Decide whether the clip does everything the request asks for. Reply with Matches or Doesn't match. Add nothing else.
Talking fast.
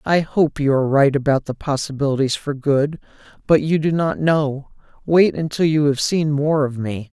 Doesn't match